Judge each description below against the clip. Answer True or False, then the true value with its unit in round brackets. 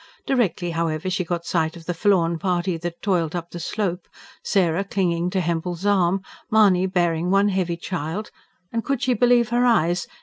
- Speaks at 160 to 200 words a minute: True (175 wpm)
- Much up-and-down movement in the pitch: False (2.9 semitones)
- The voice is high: False (180 Hz)